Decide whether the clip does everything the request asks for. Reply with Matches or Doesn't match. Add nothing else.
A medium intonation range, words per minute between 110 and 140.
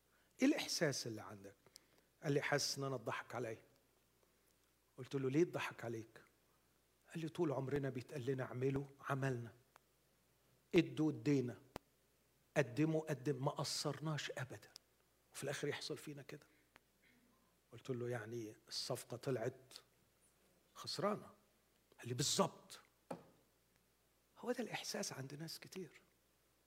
Matches